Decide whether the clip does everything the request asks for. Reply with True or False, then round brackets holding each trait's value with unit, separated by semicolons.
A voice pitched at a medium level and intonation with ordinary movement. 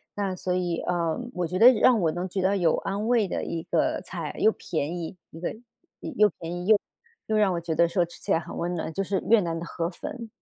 True (180 Hz; 3.1 semitones)